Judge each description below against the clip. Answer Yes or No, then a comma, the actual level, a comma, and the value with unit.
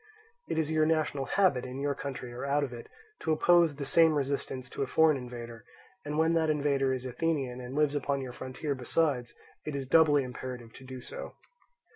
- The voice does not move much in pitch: No, average, 3.3 semitones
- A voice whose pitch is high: No, medium, 140 Hz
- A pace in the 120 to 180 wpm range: No, average, 200 wpm